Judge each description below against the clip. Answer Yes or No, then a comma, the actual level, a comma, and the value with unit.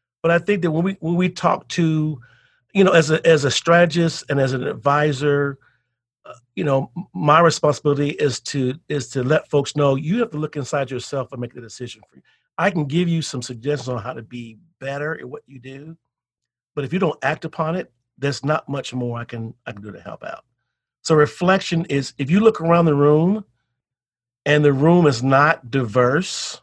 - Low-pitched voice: No, medium, 145 Hz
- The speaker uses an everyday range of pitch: Yes, average, 4.5 semitones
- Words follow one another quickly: Yes, fast, 210 wpm